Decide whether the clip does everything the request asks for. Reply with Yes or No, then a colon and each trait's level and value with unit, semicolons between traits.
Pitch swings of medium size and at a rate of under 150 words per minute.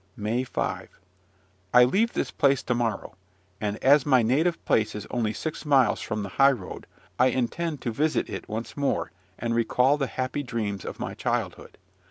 No: average, 4.1 semitones; average, 180 wpm